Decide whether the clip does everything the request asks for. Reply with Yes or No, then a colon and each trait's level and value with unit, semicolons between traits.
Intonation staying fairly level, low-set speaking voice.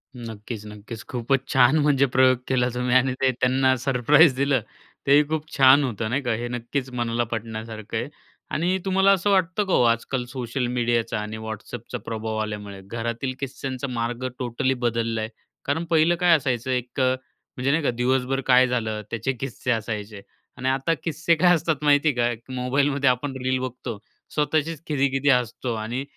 No: average, 3.0 semitones; low, 130 Hz